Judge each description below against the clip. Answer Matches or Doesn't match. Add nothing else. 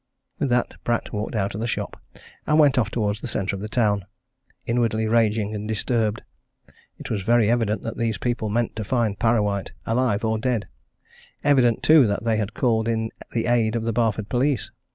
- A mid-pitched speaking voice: Doesn't match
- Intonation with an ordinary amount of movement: Doesn't match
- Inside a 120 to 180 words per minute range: Doesn't match